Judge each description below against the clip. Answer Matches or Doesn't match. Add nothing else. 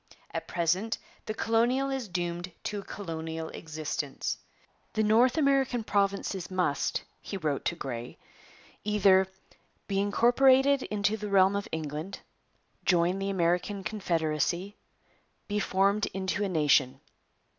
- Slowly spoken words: Matches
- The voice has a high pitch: Matches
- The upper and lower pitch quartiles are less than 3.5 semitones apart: Doesn't match